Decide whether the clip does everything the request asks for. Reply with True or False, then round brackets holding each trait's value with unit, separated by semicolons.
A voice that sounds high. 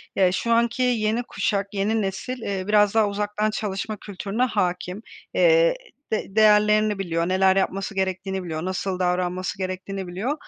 True (200 Hz)